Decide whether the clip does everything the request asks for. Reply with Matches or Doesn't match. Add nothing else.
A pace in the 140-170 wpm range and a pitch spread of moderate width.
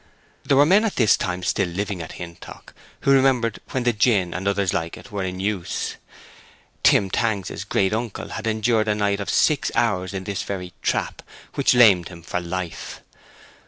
Doesn't match